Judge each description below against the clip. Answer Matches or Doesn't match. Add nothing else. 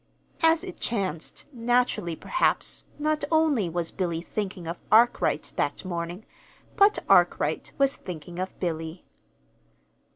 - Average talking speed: Doesn't match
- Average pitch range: Doesn't match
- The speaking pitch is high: Matches